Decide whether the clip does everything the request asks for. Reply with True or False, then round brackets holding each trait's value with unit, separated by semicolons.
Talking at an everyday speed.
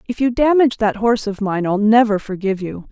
False (225 wpm)